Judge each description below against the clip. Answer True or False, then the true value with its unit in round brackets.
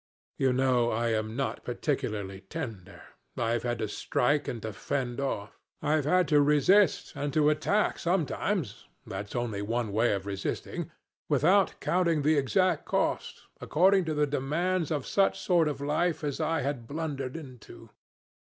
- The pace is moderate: True (155 wpm)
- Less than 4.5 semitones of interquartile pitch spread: False (5.3 semitones)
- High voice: False (140 Hz)